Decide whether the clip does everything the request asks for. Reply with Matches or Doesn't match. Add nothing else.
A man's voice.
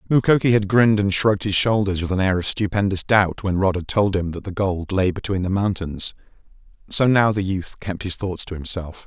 Matches